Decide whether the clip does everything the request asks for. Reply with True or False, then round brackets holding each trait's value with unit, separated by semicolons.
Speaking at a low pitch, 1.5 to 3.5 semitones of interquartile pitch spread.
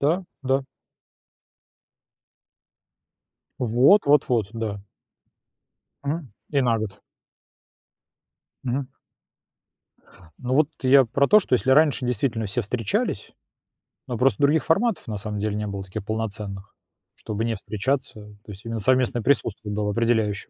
False (115 Hz; 4.3 semitones)